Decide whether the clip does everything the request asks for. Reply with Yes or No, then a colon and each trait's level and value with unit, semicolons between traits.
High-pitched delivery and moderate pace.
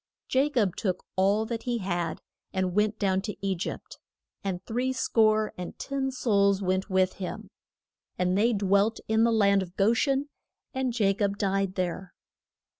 Yes: high, 200 Hz; average, 170 wpm